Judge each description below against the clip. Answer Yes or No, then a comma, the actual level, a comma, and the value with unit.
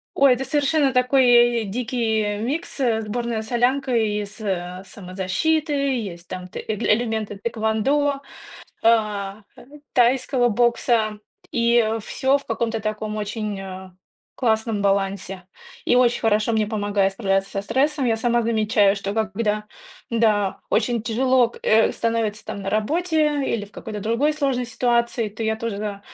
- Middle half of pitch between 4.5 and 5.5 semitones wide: No, average, 2.9 semitones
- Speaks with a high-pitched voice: Yes, high, 225 Hz